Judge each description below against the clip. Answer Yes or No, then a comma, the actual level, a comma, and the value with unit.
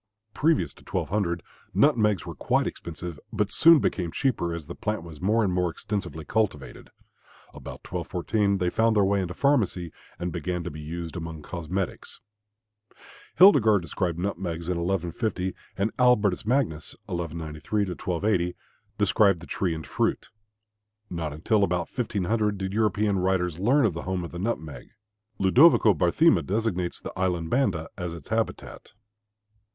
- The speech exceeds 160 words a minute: No, average, 145 wpm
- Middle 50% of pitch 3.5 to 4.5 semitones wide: Yes, average, 3.8 semitones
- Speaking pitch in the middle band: No, very low, 95 Hz